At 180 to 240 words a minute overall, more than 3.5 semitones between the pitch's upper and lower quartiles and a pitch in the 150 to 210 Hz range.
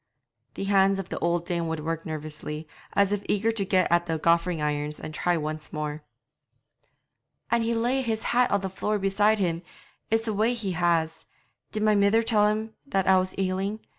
Yes: average, 195 wpm; average, 4.4 semitones; high, 190 Hz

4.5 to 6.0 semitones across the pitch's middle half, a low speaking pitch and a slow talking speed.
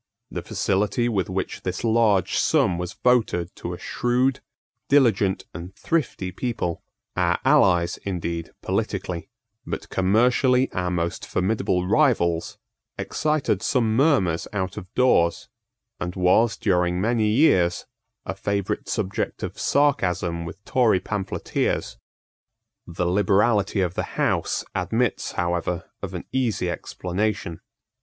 Yes: average, 4.8 semitones; very low, 95 Hz; slow, 120 wpm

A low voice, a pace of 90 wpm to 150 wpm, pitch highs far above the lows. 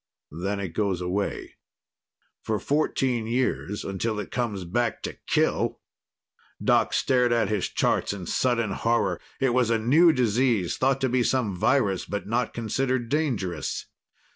No: low, 115 Hz; average, 145 wpm; average, 4.2 semitones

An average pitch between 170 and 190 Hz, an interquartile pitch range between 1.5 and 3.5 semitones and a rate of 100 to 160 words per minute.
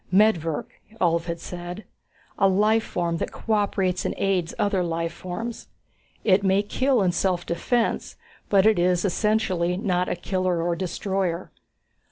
Yes: medium, 185 Hz; average, 2.8 semitones; average, 145 wpm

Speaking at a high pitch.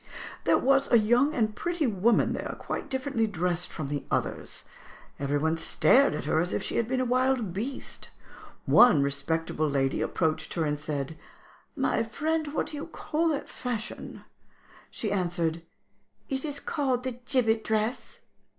Yes: high, 225 Hz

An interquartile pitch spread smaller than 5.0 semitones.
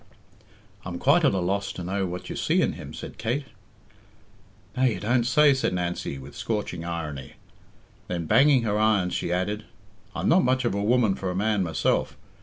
No: wide, 5.4 semitones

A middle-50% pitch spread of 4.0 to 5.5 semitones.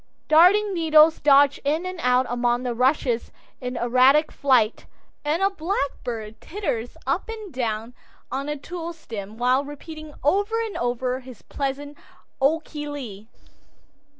Yes: average, 4.6 semitones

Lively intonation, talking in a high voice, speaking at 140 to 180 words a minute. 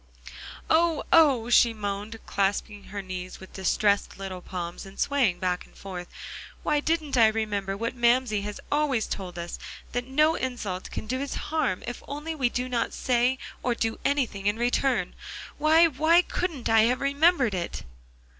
Yes: wide, 5.9 semitones; high, 235 Hz; average, 165 wpm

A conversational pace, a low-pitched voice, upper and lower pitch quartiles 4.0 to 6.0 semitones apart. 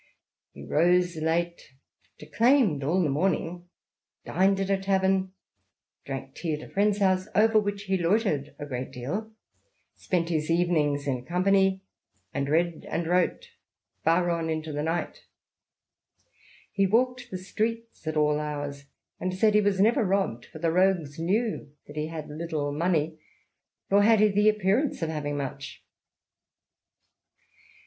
No: average, 150 wpm; medium, 175 Hz; average, 4.4 semitones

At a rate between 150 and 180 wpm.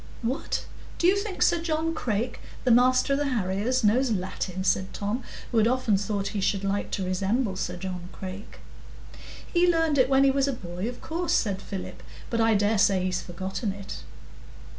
No: average, 190 wpm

